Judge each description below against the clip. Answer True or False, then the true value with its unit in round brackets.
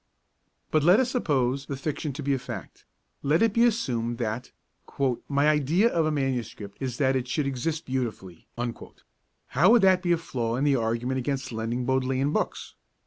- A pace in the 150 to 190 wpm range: True (180 wpm)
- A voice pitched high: False (135 Hz)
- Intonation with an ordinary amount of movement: True (3.8 semitones)